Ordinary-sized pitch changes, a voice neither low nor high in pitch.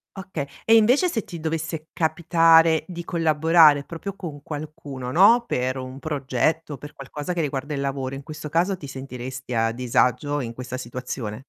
Yes: average, 3.9 semitones; medium, 150 Hz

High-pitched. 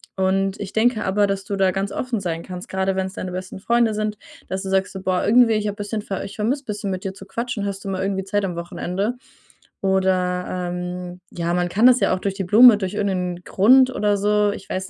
Yes: high, 195 Hz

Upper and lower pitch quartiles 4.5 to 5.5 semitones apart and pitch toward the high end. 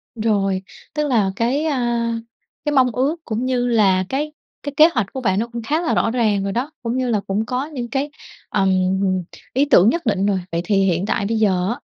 Yes: average, 4.9 semitones; high, 230 Hz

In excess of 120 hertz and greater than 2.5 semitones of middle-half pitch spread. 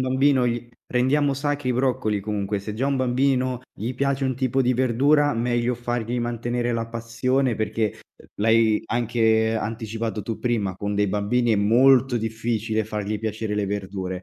No: low, 115 Hz; average, 2.9 semitones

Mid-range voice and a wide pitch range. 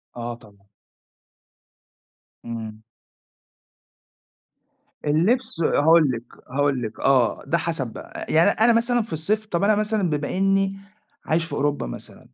Yes: medium, 160 Hz; wide, 7.8 semitones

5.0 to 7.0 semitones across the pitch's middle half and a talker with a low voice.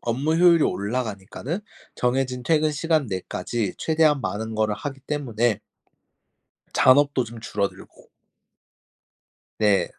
Yes: average, 5.3 semitones; low, 125 Hz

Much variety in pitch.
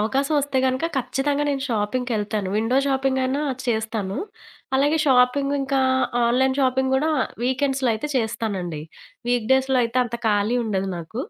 No: average, 3.4 semitones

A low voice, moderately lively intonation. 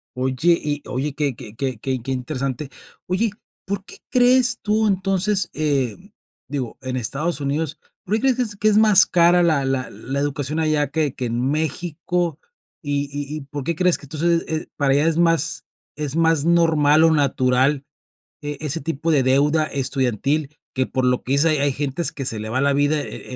No: medium, 150 Hz; average, 3.7 semitones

